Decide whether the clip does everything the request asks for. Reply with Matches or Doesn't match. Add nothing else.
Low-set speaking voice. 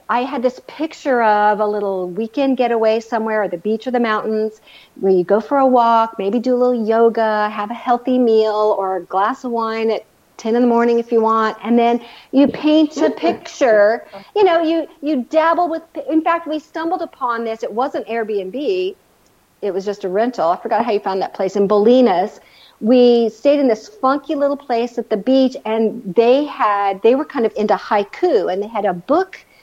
Doesn't match